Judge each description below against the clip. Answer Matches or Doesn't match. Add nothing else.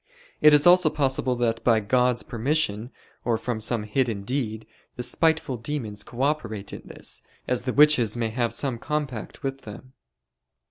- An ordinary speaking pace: Matches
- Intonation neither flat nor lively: Matches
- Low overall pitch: Matches